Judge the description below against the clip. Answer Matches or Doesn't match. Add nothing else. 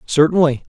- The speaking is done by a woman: Doesn't match